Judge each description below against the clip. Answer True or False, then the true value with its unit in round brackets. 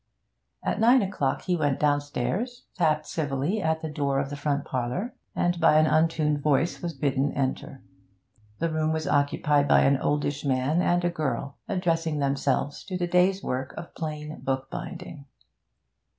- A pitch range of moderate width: True (3.4 semitones)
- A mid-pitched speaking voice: True (150 Hz)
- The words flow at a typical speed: True (160 wpm)